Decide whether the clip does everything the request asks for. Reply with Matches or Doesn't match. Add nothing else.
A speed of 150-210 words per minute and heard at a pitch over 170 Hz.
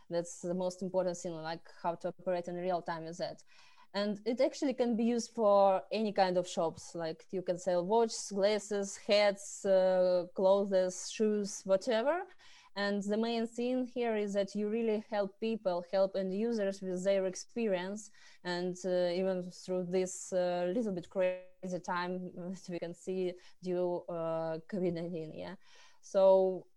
Matches